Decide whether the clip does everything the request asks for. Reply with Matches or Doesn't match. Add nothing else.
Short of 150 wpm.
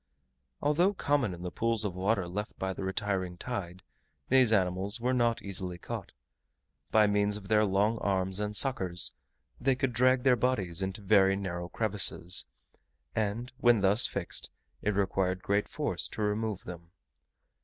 Doesn't match